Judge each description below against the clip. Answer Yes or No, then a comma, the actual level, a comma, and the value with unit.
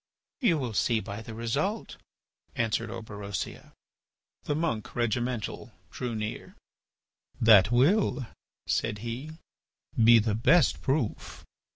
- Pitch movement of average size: Yes, average, 3.7 semitones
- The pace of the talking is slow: Yes, slow, 105 wpm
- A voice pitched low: Yes, low, 115 Hz